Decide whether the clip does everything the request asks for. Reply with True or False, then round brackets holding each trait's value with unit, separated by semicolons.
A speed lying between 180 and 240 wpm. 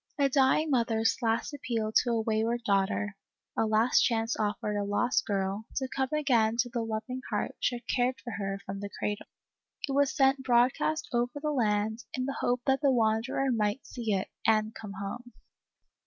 True (185 wpm)